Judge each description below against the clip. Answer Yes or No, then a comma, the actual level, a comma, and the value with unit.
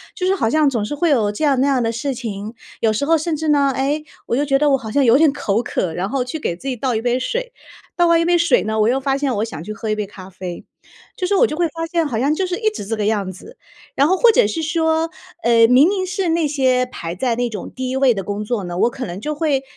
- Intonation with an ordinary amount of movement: No, wide, 6.4 semitones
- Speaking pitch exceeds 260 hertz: Yes, very high, 270 Hz